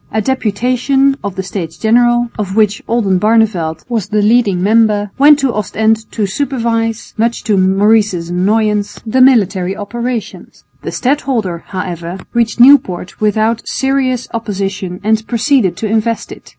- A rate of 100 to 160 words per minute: Yes, slow, 135 wpm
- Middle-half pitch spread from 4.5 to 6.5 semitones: No, average, 3.4 semitones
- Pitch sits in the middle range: No, high, 220 Hz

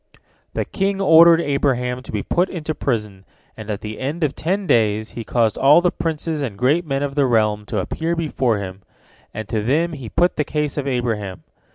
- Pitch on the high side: No, low, 135 Hz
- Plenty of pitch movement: Yes, wide, 6.7 semitones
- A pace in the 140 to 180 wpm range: No, fast, 205 wpm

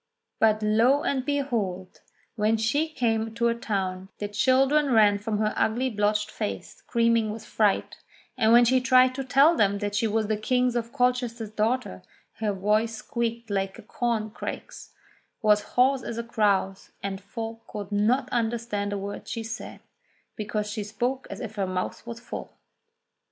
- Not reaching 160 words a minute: No, average, 165 wpm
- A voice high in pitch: Yes, high, 225 Hz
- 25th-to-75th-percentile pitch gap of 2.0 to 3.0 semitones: Yes, average, 2.7 semitones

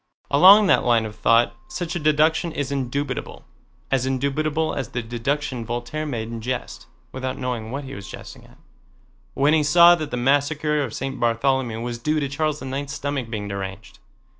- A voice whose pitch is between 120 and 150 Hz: Yes, low, 135 Hz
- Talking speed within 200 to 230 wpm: No, average, 180 wpm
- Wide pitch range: No, average, 4.0 semitones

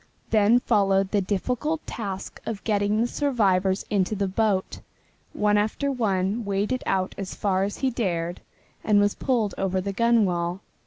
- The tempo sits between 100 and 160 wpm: Yes, average, 155 wpm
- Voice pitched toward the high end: Yes, high, 205 Hz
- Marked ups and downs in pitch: No, average, 2.9 semitones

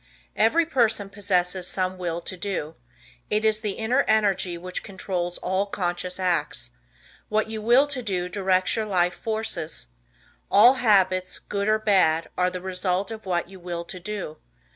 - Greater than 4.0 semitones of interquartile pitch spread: No, average, 3.1 semitones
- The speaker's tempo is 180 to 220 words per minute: No, average, 165 wpm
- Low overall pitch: No, high, 190 Hz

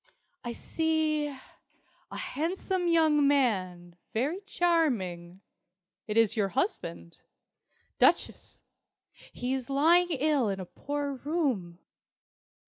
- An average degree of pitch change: No, wide, 8.0 semitones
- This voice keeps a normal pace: No, slow, 100 wpm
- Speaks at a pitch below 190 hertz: No, very high, 275 Hz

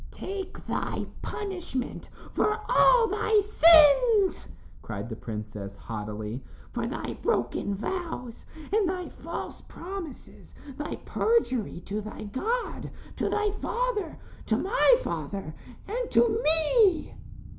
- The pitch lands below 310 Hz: No, very high, 345 Hz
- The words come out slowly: Yes, slow, 115 wpm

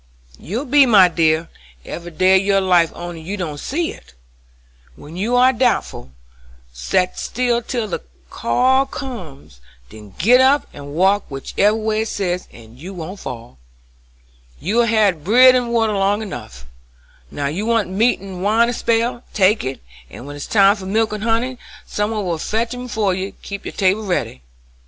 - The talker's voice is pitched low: No, high, 200 Hz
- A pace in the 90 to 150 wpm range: No, average, 175 wpm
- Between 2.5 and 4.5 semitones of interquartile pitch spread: No, average, 5.2 semitones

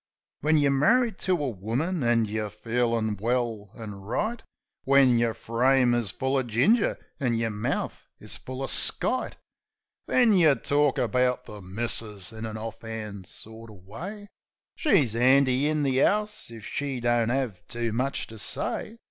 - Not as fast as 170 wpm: Yes, average, 160 wpm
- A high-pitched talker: No, low, 120 Hz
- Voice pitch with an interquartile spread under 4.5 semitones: Yes, average, 4.0 semitones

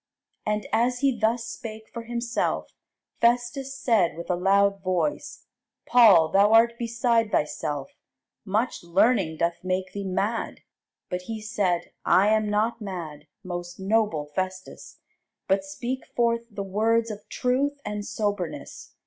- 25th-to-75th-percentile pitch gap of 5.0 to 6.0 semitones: No, average, 3.9 semitones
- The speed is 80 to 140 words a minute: Yes, slow, 135 wpm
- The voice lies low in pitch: No, high, 210 Hz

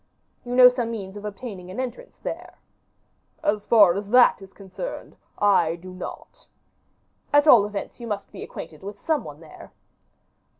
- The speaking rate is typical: Yes, average, 165 wpm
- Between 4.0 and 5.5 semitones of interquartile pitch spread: Yes, average, 4.4 semitones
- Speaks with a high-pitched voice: Yes, high, 205 Hz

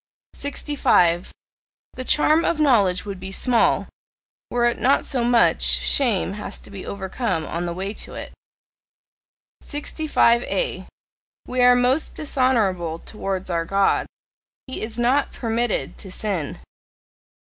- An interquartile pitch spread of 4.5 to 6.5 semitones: Yes, average, 5.2 semitones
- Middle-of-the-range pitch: No, high, 230 Hz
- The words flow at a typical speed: No, slow, 125 wpm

